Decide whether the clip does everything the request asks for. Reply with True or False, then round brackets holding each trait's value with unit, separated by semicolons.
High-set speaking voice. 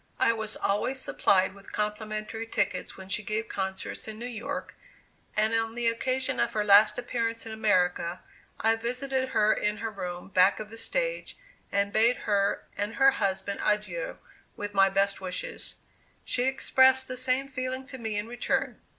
True (220 Hz)